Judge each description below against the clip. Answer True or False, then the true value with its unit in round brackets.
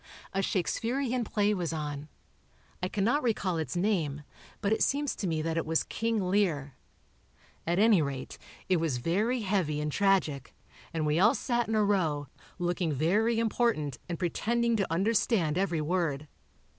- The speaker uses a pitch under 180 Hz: False (185 Hz)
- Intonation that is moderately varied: False (5.7 semitones)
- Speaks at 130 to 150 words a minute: False (160 wpm)